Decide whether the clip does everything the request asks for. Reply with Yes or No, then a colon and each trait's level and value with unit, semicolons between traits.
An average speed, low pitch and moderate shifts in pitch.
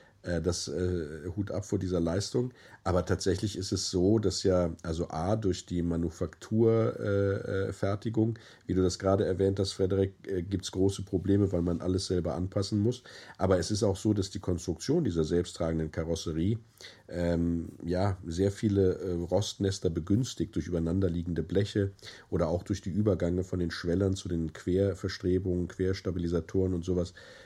No: average, 160 wpm; very low, 95 Hz; narrow, 2.3 semitones